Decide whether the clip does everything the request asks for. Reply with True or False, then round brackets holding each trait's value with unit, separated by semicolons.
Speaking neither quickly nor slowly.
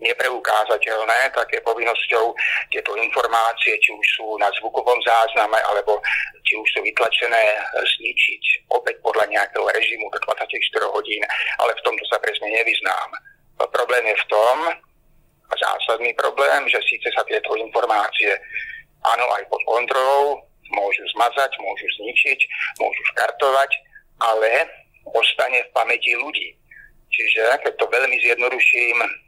True (130 wpm)